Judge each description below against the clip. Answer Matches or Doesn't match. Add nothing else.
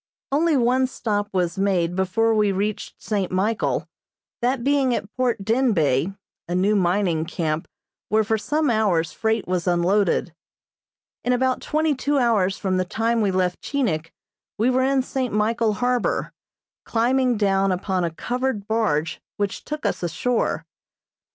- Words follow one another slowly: Doesn't match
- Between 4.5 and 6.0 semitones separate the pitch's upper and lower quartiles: Matches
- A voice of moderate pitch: Doesn't match